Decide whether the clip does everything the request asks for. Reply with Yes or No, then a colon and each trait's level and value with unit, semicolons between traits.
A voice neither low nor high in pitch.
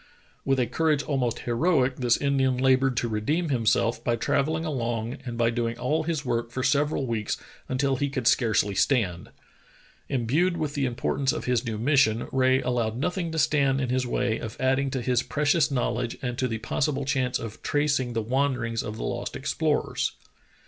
No: low, 130 Hz